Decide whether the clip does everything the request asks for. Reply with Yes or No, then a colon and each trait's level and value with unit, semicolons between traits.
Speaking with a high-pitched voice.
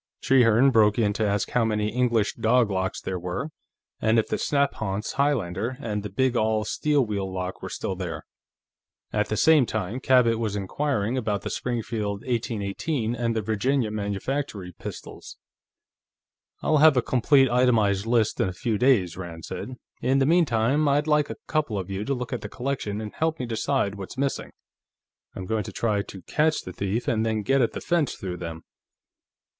No: low, 115 Hz